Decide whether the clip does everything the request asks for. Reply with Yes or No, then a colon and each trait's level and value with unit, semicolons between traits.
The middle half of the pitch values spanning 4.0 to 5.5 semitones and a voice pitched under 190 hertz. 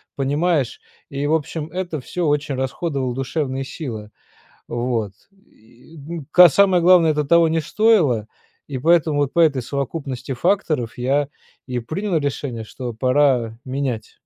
Yes: average, 4.4 semitones; medium, 140 Hz